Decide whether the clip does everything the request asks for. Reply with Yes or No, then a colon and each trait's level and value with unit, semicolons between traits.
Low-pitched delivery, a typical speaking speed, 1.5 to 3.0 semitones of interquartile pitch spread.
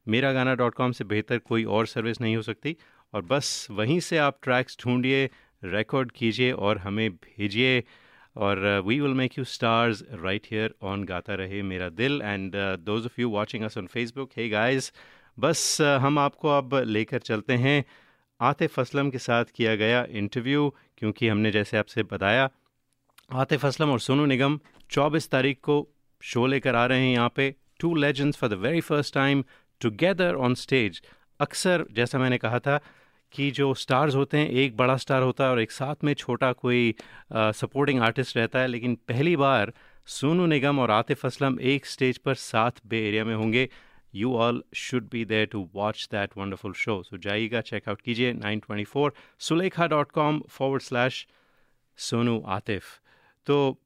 No: low, 125 Hz; average, 175 wpm; average, 3.9 semitones